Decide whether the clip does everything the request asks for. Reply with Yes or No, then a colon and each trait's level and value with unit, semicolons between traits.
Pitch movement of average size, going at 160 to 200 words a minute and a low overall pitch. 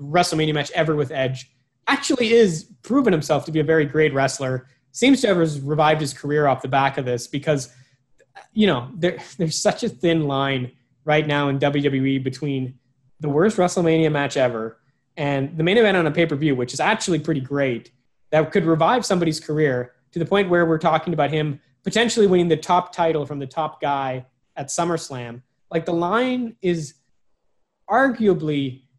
No: average, 4.3 semitones; average, 180 wpm; medium, 150 Hz